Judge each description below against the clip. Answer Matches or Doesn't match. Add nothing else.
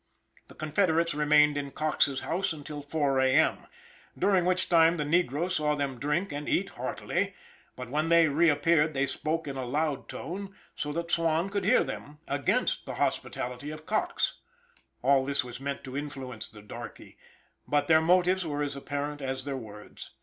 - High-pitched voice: Doesn't match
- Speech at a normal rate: Matches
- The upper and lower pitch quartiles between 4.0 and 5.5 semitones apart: Doesn't match